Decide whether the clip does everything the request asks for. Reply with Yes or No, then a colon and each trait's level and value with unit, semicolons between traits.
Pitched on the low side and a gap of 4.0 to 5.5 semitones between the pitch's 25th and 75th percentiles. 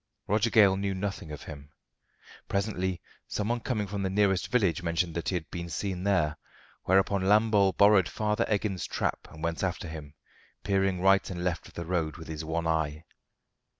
No: very low, 95 Hz; average, 3.3 semitones